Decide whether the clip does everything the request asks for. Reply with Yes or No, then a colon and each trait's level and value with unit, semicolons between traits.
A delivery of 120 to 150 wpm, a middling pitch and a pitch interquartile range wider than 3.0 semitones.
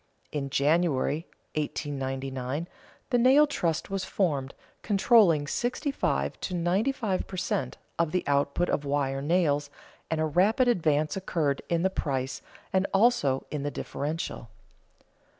Yes: slow, 135 wpm; medium, 160 Hz; average, 5.1 semitones